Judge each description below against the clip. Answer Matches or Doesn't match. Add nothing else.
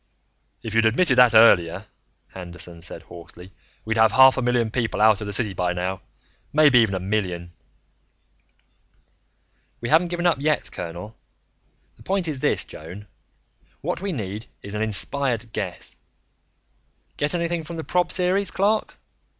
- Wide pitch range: Matches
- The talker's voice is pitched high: Doesn't match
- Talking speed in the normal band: Matches